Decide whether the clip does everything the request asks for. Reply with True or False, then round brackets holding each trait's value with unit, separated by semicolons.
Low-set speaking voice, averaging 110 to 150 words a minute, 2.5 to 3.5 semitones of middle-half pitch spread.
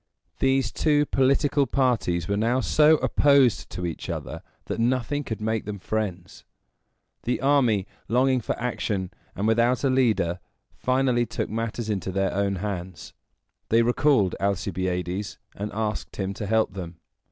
False (110 Hz; 145 wpm; 4.8 semitones)